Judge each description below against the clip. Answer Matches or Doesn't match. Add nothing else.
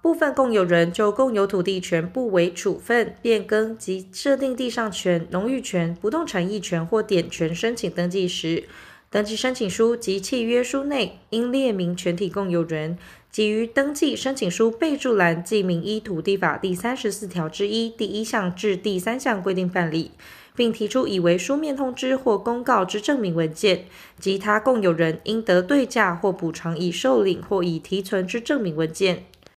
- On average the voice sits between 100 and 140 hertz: Doesn't match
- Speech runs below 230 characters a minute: Doesn't match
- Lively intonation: Doesn't match